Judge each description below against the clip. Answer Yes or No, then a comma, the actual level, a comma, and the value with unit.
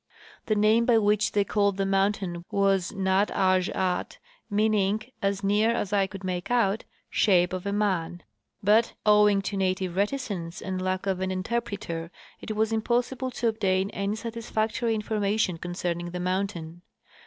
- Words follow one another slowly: No, average, 165 wpm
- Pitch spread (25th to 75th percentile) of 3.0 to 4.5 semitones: No, narrow, 2.5 semitones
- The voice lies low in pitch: No, high, 200 Hz